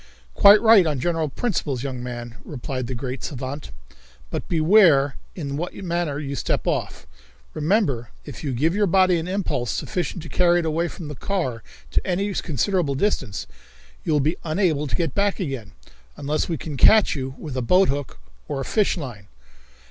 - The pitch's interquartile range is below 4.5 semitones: No, average, 5.2 semitones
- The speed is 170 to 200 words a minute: Yes, average, 175 wpm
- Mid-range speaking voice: Yes, medium, 155 Hz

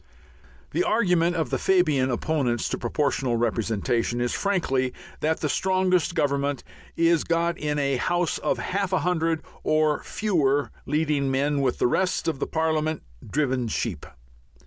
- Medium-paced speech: Yes, average, 145 wpm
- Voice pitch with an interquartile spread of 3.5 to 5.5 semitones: Yes, average, 4.3 semitones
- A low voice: No, medium, 150 Hz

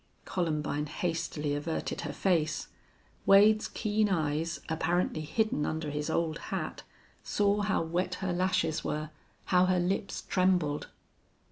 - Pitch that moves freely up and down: No, average, 3.5 semitones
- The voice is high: No, medium, 170 Hz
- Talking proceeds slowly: Yes, slow, 125 wpm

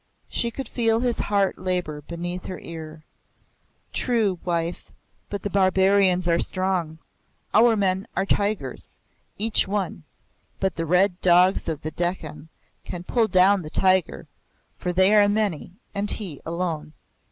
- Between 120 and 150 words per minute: Yes, average, 140 wpm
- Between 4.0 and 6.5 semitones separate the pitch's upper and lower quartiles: No, average, 3.1 semitones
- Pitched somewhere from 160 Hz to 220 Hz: Yes, medium, 185 Hz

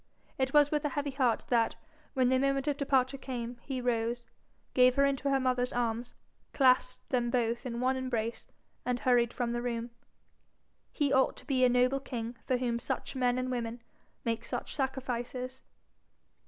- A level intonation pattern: Yes, narrow, 1.8 semitones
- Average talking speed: Yes, average, 175 wpm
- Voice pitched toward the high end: Yes, very high, 255 Hz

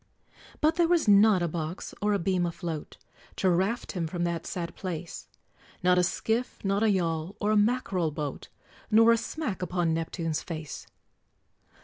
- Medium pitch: Yes, medium, 180 Hz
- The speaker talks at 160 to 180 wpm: Yes, average, 165 wpm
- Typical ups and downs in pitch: Yes, average, 4.1 semitones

